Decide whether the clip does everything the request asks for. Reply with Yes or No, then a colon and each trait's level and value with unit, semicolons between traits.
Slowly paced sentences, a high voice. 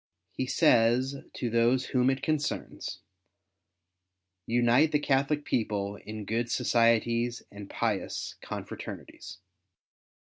No: slow, 105 wpm; low, 115 Hz